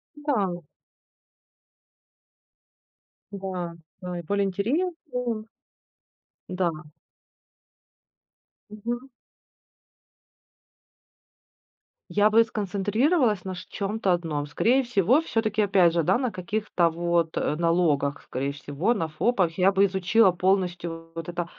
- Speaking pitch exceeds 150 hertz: Yes, high, 190 Hz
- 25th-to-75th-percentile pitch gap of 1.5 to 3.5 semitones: No, average, 4.3 semitones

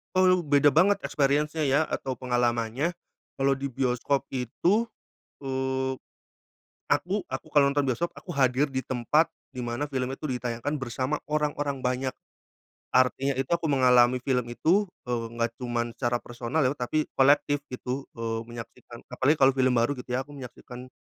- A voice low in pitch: Yes, low, 130 Hz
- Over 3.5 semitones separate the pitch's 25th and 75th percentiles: No, average, 2.7 semitones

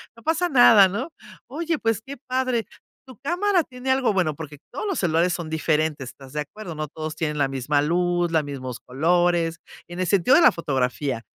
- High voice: No, medium, 175 Hz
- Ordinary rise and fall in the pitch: No, wide, 8.8 semitones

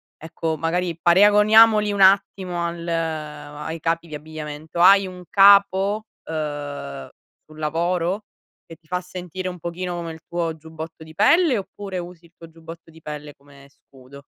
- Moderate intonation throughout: Yes, average, 3.0 semitones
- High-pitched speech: No, medium, 170 Hz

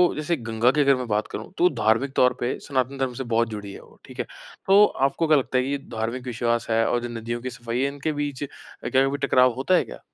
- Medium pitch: No, low, 130 Hz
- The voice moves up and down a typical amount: Yes, average, 3.0 semitones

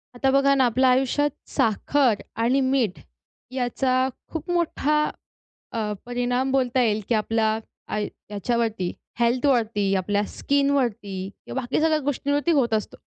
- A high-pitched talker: Yes, high, 245 Hz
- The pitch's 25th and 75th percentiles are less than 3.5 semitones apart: No, average, 3.9 semitones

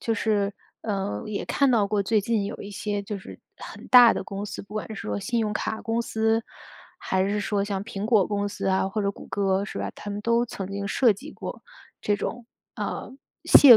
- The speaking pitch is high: Yes, high, 205 Hz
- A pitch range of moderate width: No, narrow, 2.1 semitones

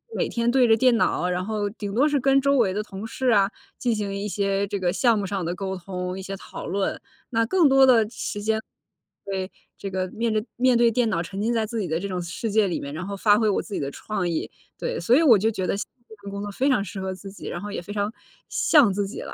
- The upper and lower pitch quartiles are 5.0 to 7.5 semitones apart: No, average, 3.3 semitones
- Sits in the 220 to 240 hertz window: No, high, 205 Hz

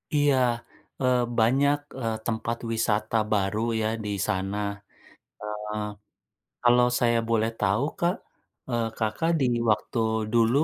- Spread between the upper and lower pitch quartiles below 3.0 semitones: Yes, narrow, 2.5 semitones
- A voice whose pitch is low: Yes, low, 115 Hz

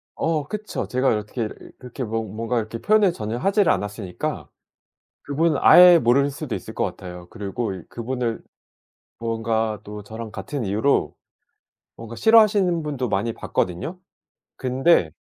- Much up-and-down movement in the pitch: Yes, wide, 5.8 semitones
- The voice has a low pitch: Yes, low, 115 Hz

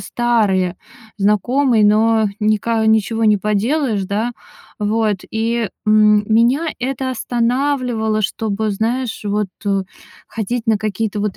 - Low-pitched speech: No, high, 220 Hz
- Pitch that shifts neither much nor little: No, narrow, 2.3 semitones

